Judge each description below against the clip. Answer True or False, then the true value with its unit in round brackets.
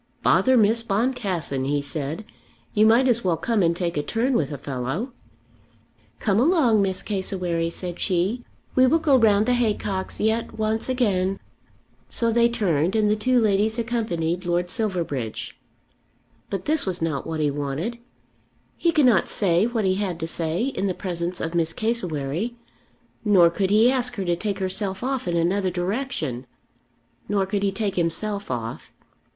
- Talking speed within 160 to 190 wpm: True (170 wpm)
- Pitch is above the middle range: True (195 Hz)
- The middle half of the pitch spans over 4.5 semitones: True (5.2 semitones)